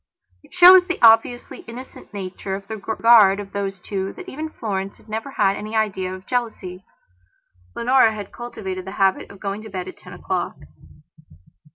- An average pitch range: Yes, average, 3.4 semitones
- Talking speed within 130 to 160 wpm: No, average, 175 wpm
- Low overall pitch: No, high, 210 Hz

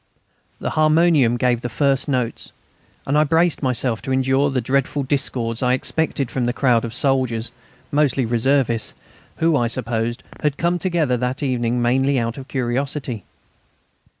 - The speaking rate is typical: Yes, average, 150 wpm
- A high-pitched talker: No, low, 130 Hz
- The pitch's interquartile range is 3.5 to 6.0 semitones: No, average, 3.0 semitones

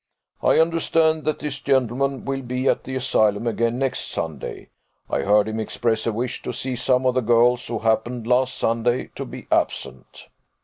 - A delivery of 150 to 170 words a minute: No, average, 180 wpm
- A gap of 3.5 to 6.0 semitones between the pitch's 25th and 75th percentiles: No, average, 2.7 semitones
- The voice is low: Yes, low, 125 Hz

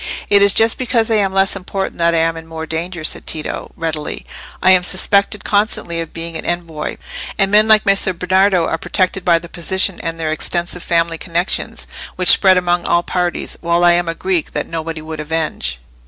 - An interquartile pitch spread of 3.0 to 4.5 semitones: No, narrow, 2.6 semitones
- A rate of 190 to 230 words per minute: Yes, average, 200 wpm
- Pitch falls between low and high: Yes, medium, 175 Hz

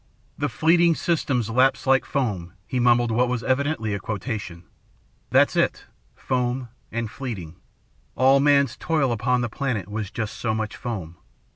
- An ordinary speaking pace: Yes, average, 150 wpm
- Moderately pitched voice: No, low, 120 Hz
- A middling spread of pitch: Yes, average, 3.6 semitones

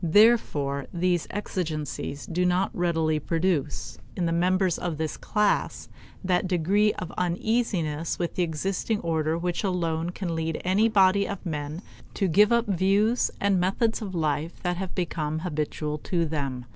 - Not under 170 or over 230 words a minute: No, average, 155 wpm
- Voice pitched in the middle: Yes, medium, 175 Hz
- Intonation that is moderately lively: Yes, average, 3.5 semitones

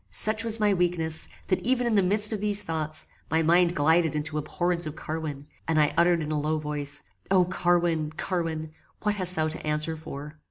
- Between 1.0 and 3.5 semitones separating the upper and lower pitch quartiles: Yes, average, 3.0 semitones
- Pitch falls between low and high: Yes, medium, 165 Hz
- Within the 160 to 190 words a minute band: No, average, 200 wpm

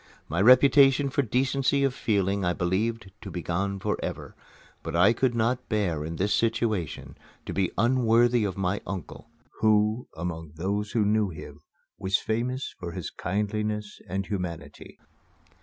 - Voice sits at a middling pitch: No, low, 105 Hz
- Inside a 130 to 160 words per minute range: Yes, average, 150 wpm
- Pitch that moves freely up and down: No, average, 4.2 semitones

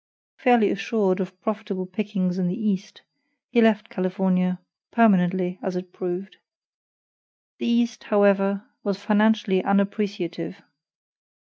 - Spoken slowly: Yes, slow, 110 wpm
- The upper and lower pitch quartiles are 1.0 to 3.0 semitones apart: Yes, narrow, 2.5 semitones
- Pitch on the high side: Yes, high, 195 Hz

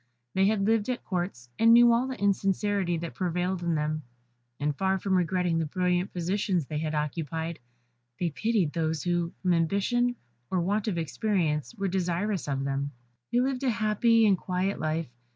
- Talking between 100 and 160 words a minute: No, average, 175 wpm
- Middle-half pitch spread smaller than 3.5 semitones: No, average, 4.0 semitones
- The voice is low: No, medium, 180 Hz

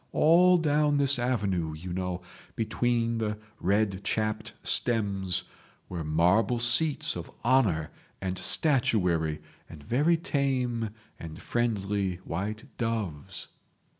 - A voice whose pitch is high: No, low, 110 Hz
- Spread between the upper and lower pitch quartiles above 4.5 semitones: Yes, average, 5.3 semitones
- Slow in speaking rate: Yes, slow, 105 wpm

